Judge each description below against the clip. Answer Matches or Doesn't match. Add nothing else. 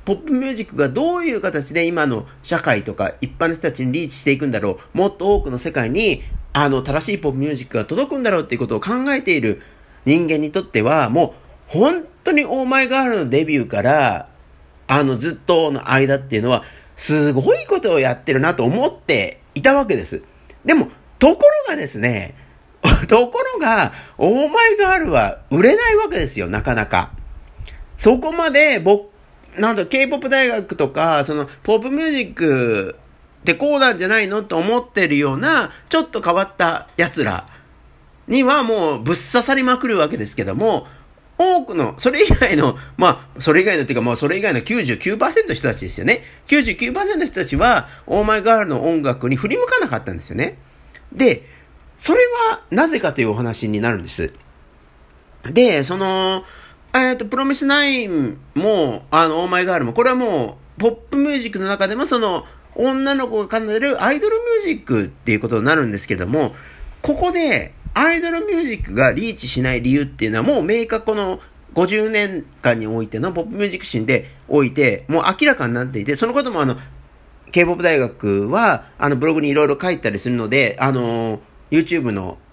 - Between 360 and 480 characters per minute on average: Matches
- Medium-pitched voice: Matches